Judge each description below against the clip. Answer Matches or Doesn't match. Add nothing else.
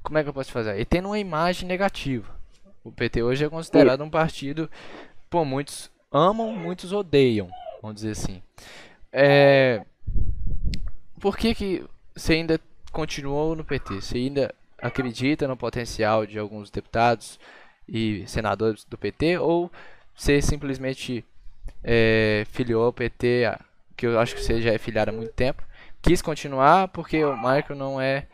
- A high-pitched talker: Doesn't match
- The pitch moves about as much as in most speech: Doesn't match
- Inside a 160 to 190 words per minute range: Doesn't match